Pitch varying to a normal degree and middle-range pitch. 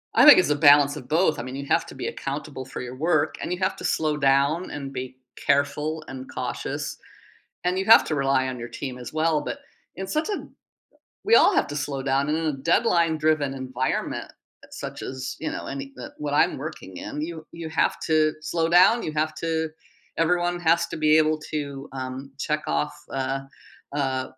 Yes: average, 3.1 semitones; medium, 150 Hz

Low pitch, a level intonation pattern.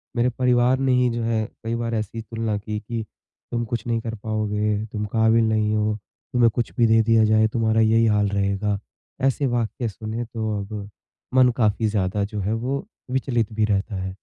Yes: low, 110 Hz; narrow, 1.8 semitones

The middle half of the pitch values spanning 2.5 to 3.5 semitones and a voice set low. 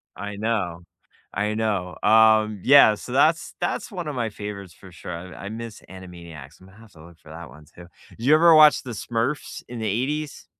No: average, 5.3 semitones; low, 105 Hz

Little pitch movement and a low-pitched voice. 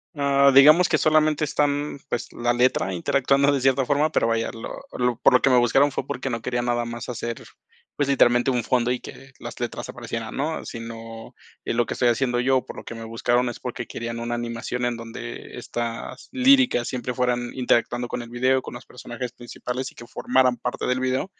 Yes: narrow, 2.2 semitones; low, 125 Hz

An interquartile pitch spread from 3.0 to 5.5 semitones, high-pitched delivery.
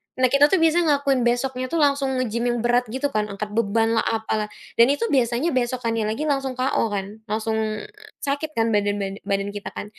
Yes: average, 3.9 semitones; high, 240 Hz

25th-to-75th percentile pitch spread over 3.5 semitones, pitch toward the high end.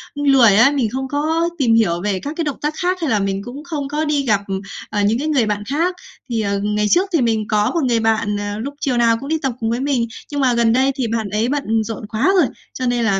Yes: average, 5.1 semitones; high, 240 Hz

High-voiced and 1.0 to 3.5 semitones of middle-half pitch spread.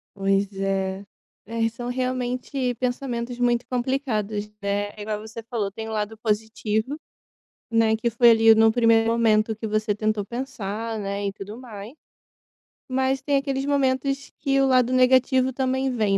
Yes: high, 230 Hz; average, 3.2 semitones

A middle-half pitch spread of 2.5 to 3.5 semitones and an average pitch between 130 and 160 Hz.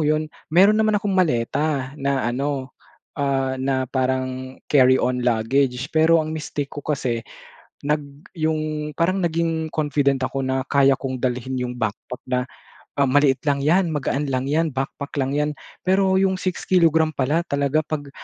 Yes: average, 3.2 semitones; medium, 140 Hz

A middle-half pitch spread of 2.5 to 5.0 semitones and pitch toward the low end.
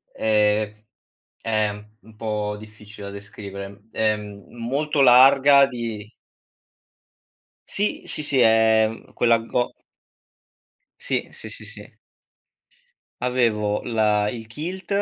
Yes: average, 2.8 semitones; low, 110 Hz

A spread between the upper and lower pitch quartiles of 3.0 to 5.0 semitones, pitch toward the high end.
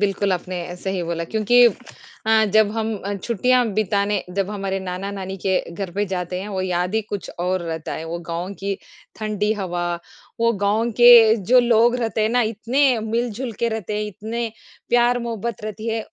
Yes: average, 3.4 semitones; high, 210 Hz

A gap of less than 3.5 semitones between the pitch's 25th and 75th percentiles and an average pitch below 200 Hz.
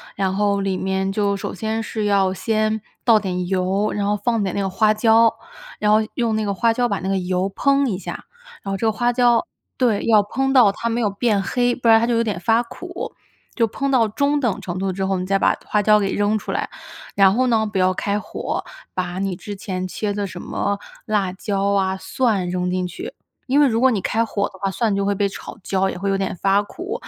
No: average, 2.8 semitones; high, 205 Hz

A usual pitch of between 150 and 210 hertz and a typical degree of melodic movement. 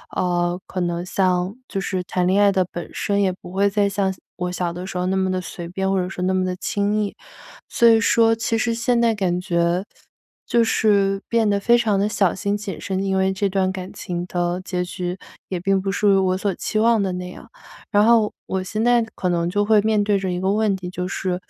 No: high, 190 Hz; narrow, 2.3 semitones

